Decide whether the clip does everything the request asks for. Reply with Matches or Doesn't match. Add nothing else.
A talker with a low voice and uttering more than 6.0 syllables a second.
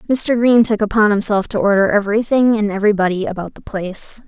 Doesn't match